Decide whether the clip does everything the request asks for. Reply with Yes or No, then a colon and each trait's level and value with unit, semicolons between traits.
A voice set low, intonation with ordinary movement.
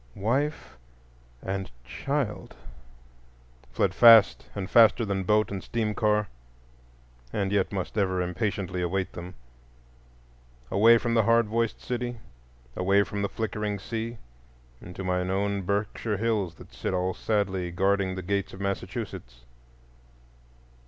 Yes: low, 100 Hz; average, 3.0 semitones